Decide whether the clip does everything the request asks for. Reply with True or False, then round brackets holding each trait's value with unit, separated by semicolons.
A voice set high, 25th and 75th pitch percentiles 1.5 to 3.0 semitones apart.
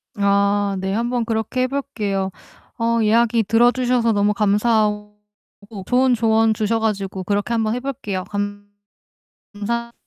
True (220 Hz; 2.6 semitones)